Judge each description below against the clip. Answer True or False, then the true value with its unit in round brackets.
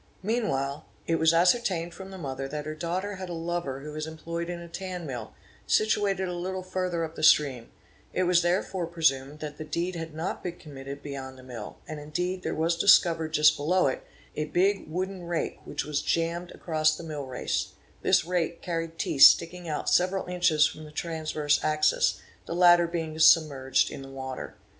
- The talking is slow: False (190 wpm)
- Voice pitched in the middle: True (165 Hz)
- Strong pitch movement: False (2.9 semitones)